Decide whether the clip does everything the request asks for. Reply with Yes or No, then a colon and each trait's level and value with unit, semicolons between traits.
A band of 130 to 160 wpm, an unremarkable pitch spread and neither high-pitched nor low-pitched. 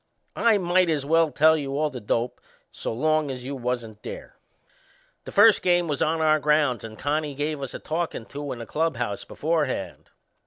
No: average, 190 wpm; average, 4.0 semitones; medium, 150 Hz